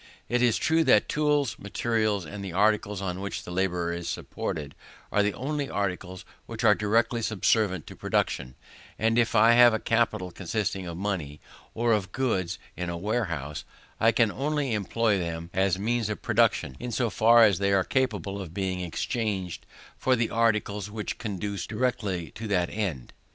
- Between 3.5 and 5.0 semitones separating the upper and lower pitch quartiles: Yes, average, 4.0 semitones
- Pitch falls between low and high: No, low, 105 Hz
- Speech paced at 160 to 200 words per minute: Yes, average, 175 wpm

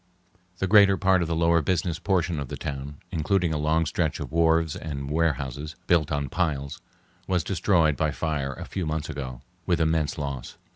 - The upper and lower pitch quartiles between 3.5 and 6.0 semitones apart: No, average, 2.8 semitones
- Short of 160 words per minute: No, average, 185 wpm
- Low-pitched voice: Yes, very low, 80 Hz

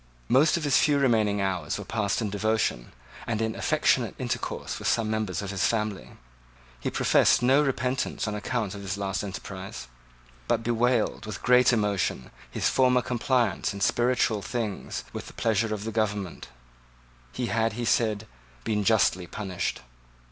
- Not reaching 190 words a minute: Yes, average, 160 wpm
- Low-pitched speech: Yes, low, 110 Hz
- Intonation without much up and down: No, average, 3.1 semitones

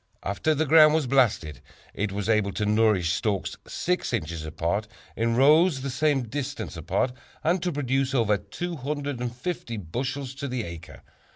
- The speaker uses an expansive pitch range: Yes, wide, 5.8 semitones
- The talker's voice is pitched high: No, low, 125 Hz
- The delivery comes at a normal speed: Yes, average, 155 wpm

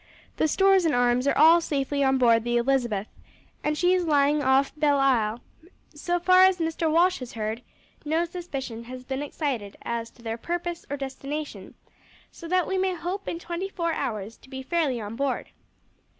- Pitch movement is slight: No, wide, 5.6 semitones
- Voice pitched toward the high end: Yes, very high, 285 Hz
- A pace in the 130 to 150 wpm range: No, average, 180 wpm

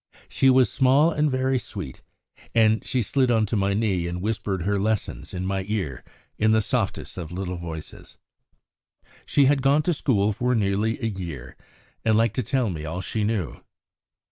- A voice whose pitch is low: Yes, low, 110 Hz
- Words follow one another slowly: No, average, 180 wpm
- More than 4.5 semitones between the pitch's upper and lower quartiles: Yes, average, 5.2 semitones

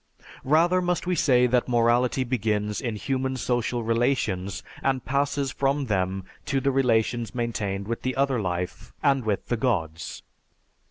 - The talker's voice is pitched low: Yes, low, 125 Hz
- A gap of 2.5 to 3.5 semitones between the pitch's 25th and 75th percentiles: No, average, 4.0 semitones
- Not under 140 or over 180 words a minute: Yes, average, 150 wpm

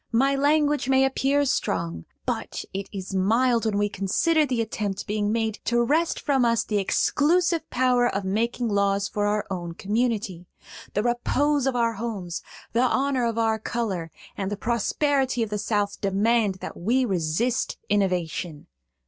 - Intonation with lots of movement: No, average, 4.3 semitones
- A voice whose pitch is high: Yes, high, 225 Hz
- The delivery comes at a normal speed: Yes, average, 160 wpm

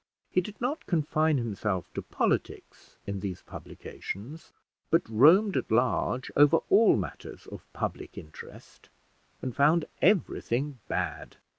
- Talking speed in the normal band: No, slow, 125 wpm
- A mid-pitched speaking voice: Yes, medium, 145 Hz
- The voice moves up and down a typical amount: No, wide, 7.3 semitones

